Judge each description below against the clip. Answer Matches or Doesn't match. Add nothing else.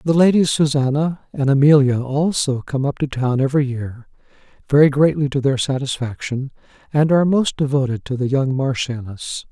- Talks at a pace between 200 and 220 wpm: Doesn't match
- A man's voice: Matches